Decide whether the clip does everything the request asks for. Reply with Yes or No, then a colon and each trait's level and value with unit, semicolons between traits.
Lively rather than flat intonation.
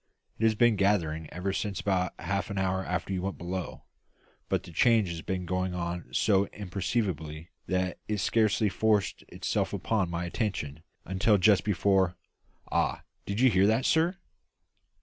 No: average, 2.8 semitones